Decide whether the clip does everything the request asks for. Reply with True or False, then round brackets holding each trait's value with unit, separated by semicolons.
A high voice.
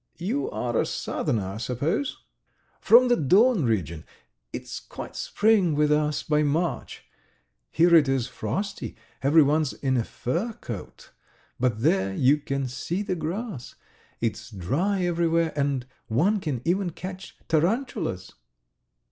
False (150 Hz)